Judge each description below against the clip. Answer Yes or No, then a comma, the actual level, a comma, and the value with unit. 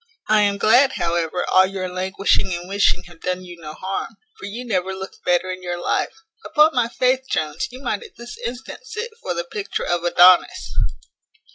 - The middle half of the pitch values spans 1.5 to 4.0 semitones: No, average, 5.2 semitones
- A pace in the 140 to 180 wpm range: No, average, 190 wpm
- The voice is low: No, high, 190 Hz